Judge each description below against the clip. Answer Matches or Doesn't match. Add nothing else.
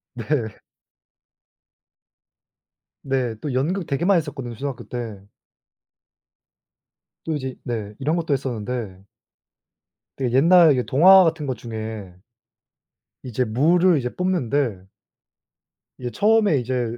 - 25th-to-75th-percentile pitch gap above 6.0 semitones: Doesn't match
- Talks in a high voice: Doesn't match